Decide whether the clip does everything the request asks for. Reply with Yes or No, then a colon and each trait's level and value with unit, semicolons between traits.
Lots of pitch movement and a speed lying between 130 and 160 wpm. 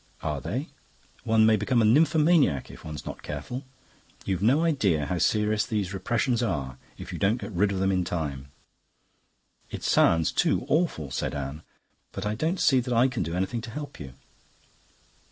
No: wide, 7.2 semitones; average, 180 wpm